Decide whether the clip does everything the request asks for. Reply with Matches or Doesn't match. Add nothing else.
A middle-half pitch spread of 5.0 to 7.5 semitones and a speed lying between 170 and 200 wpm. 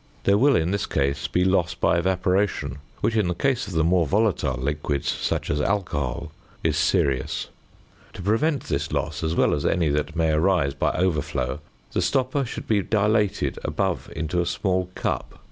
Matches